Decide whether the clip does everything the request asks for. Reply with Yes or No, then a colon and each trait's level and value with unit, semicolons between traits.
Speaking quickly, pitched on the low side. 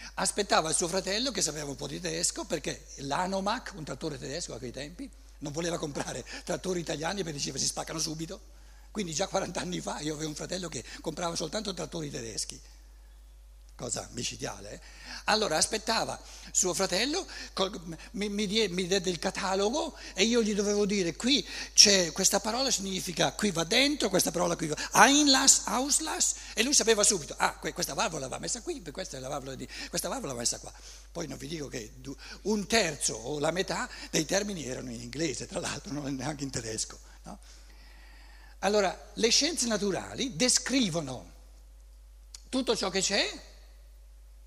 No: fast, 175 wpm; medium, 180 Hz